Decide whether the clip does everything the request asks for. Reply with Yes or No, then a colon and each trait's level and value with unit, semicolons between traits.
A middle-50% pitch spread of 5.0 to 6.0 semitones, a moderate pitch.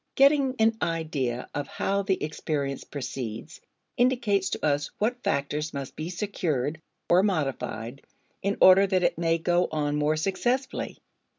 Yes: wide, 5.5 semitones; medium, 165 Hz